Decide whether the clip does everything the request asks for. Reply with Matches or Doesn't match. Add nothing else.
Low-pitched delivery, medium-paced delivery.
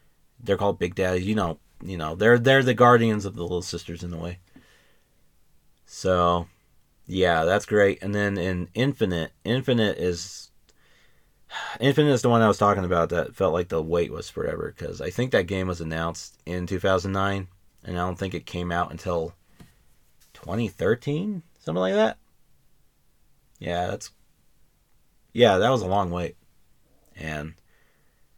Matches